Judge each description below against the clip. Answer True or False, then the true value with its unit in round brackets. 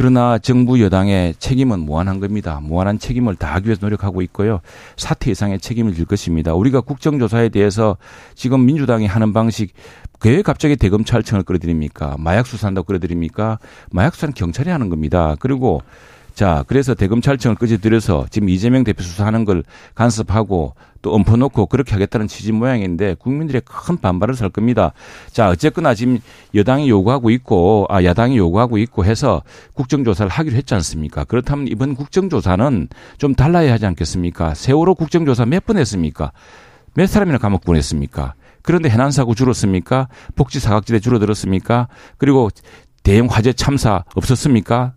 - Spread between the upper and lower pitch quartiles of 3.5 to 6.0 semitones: True (5.3 semitones)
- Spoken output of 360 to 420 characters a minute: True (405 characters per minute)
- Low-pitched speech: True (110 Hz)